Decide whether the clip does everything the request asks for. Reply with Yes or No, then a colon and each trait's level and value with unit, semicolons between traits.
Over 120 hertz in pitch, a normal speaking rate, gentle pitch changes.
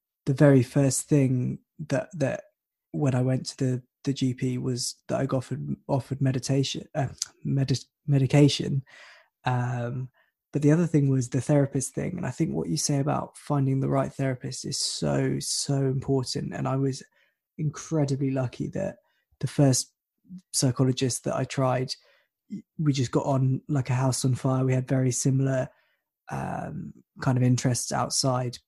Yes: low, 135 Hz; average, 160 wpm; narrow, 1.9 semitones